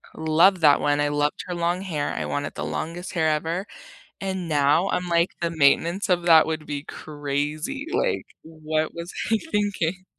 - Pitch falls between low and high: Yes, medium, 160 Hz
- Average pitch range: Yes, average, 3.3 semitones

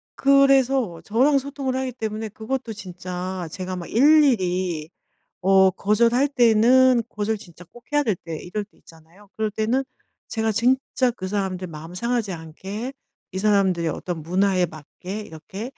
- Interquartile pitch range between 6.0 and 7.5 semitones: No, average, 5.2 semitones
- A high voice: Yes, high, 210 Hz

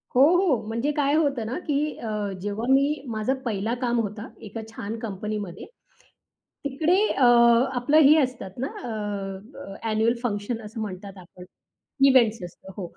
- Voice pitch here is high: Yes, high, 230 Hz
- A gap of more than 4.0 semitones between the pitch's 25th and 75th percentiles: Yes, average, 4.6 semitones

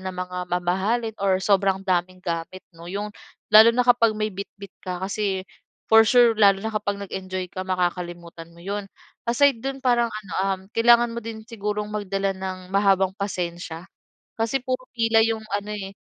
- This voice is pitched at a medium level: No, high, 200 Hz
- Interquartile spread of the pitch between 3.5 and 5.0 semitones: No, average, 3.1 semitones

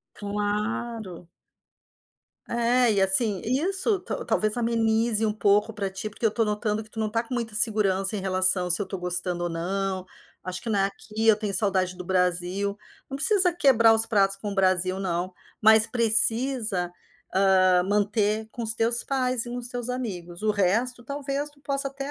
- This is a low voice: No, high, 215 Hz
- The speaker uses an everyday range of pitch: Yes, average, 3.5 semitones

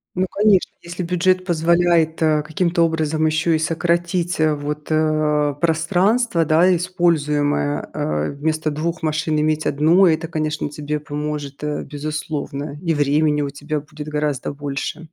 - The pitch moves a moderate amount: No, narrow, 2.3 semitones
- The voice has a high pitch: No, medium, 155 Hz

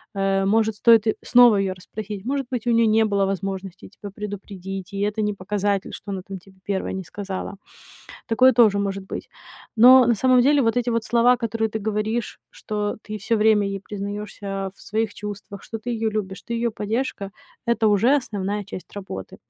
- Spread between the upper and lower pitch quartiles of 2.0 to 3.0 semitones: Yes, narrow, 2.5 semitones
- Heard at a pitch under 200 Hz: No, high, 210 Hz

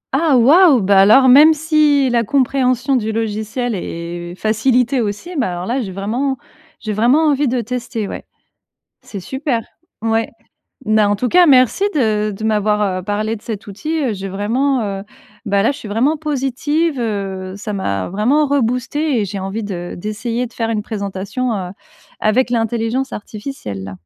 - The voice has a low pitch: No, high, 225 Hz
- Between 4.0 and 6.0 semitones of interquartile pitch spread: Yes, average, 4.6 semitones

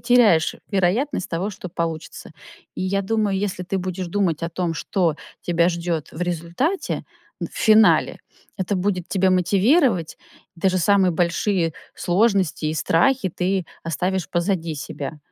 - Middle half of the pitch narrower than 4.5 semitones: Yes, average, 2.9 semitones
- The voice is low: No, medium, 185 Hz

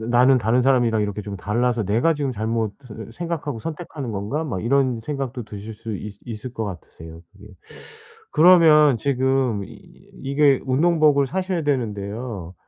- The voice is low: Yes, low, 125 Hz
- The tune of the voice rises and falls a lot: No, average, 5.0 semitones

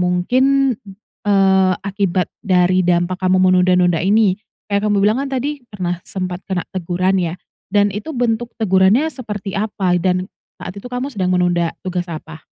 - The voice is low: No, high, 190 Hz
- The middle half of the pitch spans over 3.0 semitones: No, average, 2.7 semitones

